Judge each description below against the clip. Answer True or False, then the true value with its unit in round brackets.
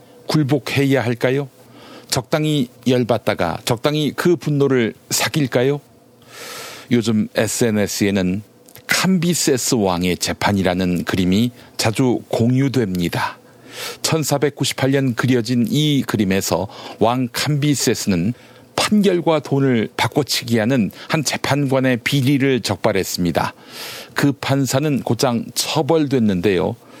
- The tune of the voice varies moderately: True (3.7 semitones)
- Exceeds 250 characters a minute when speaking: False (235 characters per minute)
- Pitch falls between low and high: False (130 Hz)